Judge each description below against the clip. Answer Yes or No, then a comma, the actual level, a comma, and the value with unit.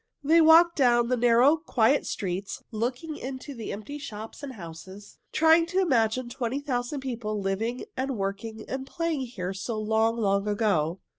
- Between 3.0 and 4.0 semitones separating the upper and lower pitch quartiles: No, average, 4.7 semitones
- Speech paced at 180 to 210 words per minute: No, average, 160 wpm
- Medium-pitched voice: No, high, 240 Hz